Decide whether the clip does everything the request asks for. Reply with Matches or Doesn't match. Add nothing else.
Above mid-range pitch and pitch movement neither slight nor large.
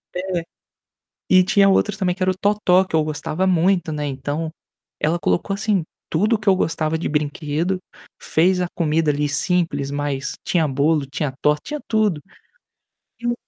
Doesn't match